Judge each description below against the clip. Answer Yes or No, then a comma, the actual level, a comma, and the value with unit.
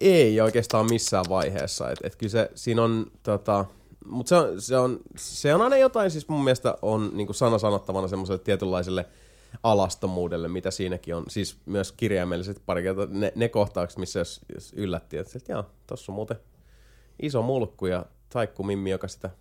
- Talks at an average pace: No, fast, 175 wpm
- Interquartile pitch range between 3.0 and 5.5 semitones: Yes, average, 3.7 semitones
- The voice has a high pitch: No, low, 100 Hz